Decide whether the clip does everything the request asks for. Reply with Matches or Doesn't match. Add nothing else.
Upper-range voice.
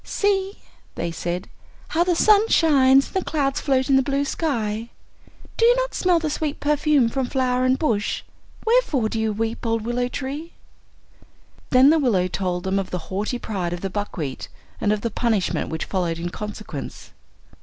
Matches